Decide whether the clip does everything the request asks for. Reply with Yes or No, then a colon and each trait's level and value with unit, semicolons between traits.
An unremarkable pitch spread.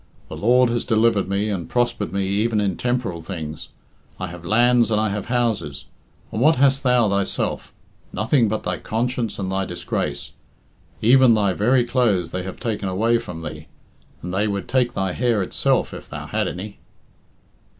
Yes: average, 4.3 semitones